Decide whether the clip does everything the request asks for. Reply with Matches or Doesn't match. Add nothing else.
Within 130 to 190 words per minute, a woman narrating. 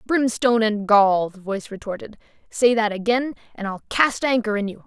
Matches